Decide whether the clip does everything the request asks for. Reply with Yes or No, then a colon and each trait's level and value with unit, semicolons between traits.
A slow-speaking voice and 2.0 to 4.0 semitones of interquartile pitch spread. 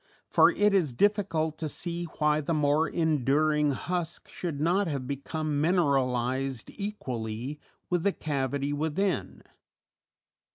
Yes: slow, 120 wpm; average, 3.7 semitones